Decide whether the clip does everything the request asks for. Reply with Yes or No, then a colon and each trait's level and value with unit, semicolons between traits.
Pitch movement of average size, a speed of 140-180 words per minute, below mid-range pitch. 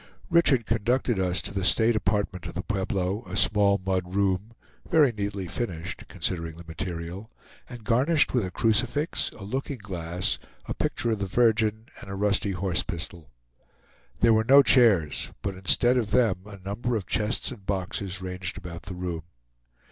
Yes: average, 3.9 semitones; average, 170 wpm; low, 100 Hz